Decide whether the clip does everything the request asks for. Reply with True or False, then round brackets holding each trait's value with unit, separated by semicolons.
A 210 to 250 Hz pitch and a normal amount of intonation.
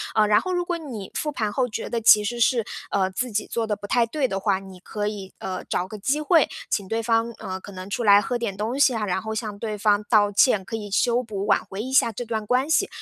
True (220 Hz; 3.1 semitones)